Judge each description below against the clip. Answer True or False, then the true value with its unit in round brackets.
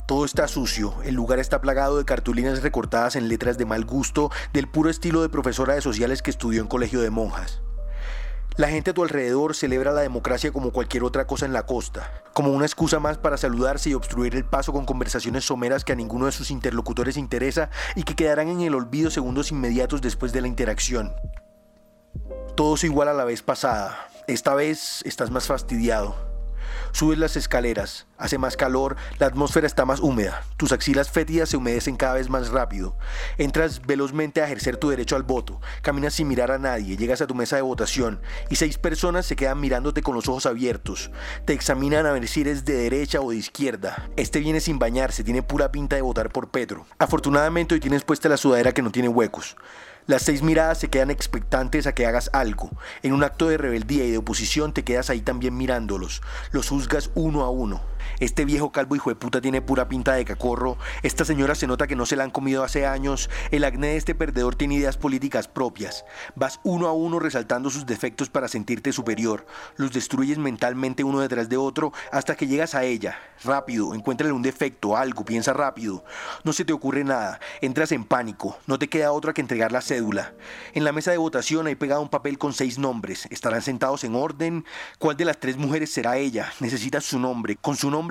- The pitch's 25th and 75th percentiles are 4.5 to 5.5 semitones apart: False (3.1 semitones)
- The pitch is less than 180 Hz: True (135 Hz)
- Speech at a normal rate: False (205 wpm)